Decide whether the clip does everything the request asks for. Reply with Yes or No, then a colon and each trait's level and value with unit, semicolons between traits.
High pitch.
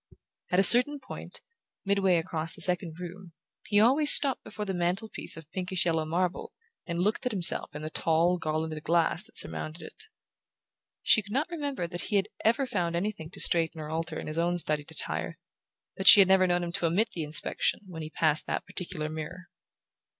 No: medium, 175 Hz